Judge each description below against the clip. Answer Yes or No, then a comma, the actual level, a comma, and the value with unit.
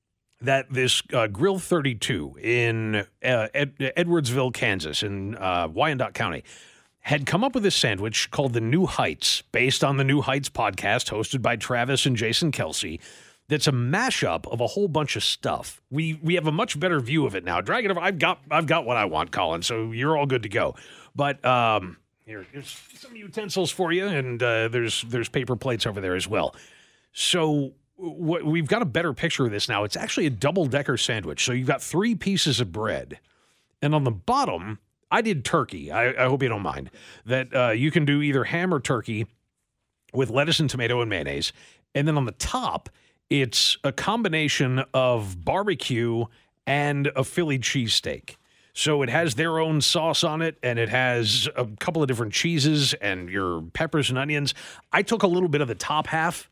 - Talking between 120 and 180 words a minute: No, average, 195 wpm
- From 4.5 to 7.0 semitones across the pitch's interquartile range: Yes, average, 5.0 semitones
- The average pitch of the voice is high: No, low, 135 Hz